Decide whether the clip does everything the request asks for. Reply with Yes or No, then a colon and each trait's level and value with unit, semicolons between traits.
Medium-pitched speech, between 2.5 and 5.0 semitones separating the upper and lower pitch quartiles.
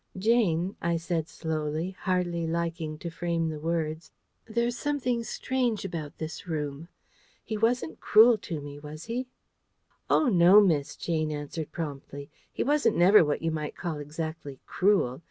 Yes: medium, 165 Hz; average, 4.7 semitones